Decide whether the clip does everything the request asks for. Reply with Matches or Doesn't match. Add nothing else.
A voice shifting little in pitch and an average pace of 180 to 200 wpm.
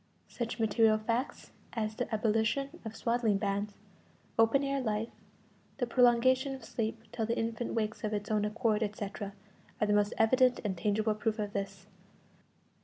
Doesn't match